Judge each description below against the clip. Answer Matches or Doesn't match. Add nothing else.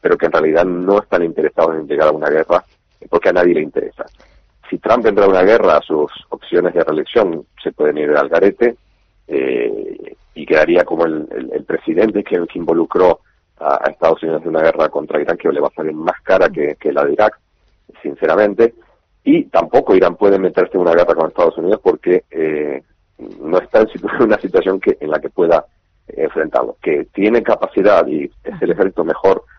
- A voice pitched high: Matches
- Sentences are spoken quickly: Matches